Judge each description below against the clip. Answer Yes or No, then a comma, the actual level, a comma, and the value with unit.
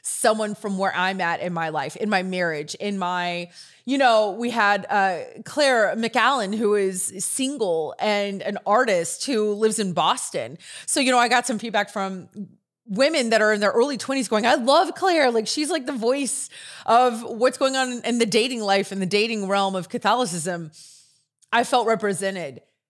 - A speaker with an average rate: Yes, average, 185 wpm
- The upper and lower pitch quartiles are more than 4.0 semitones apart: Yes, average, 4.5 semitones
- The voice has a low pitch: No, high, 215 Hz